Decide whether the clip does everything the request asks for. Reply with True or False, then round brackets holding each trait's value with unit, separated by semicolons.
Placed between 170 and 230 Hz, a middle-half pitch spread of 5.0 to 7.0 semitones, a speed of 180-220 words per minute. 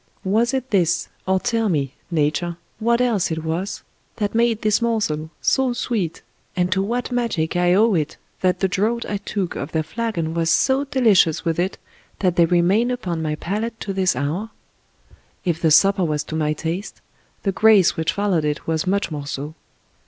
True (185 Hz; 5.4 semitones; 185 wpm)